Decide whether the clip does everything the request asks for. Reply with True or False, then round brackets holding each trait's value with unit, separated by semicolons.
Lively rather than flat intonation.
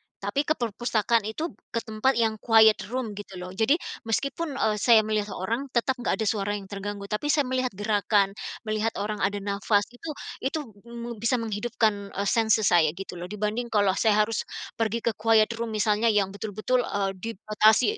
False (2.4 semitones)